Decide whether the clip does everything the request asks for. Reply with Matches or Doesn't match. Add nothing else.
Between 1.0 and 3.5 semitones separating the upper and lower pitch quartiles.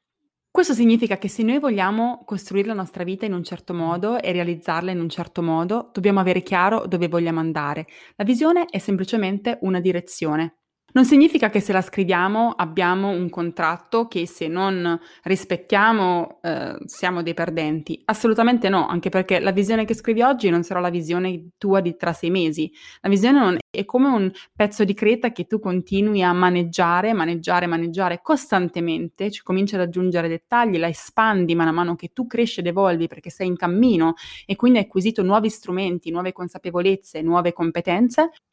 Doesn't match